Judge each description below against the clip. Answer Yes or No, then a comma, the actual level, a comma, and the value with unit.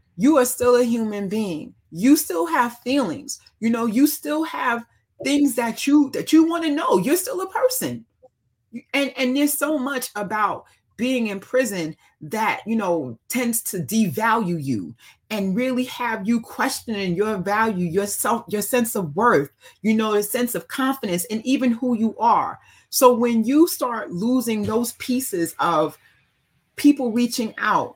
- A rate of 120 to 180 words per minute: Yes, average, 165 wpm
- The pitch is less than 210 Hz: No, high, 240 Hz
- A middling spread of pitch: Yes, average, 4.0 semitones